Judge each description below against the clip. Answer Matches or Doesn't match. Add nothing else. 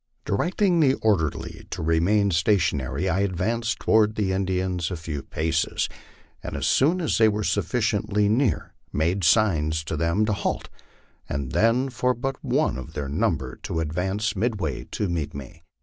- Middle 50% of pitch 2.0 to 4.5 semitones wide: Doesn't match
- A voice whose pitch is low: Matches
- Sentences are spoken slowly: Doesn't match